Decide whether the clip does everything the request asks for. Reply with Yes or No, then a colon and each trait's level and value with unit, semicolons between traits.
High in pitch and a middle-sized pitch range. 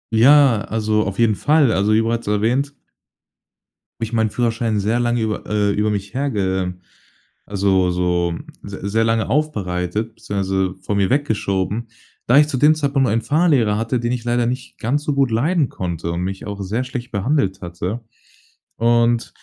No: low, 110 Hz; average, 4.0 semitones